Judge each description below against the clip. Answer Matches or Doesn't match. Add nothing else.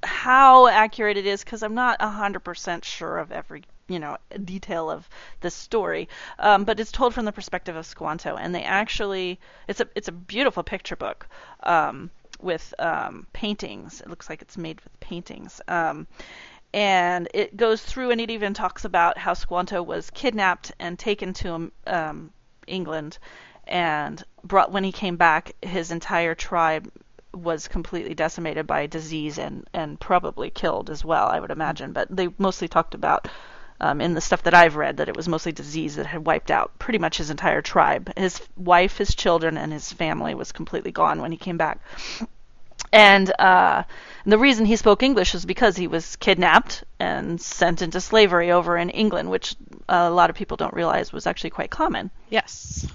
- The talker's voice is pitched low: Doesn't match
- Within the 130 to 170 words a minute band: Doesn't match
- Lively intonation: Doesn't match